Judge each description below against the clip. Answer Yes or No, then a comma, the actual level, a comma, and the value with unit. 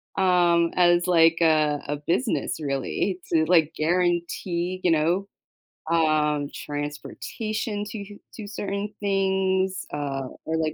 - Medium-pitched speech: Yes, medium, 175 Hz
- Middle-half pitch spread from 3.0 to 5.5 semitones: Yes, average, 3.7 semitones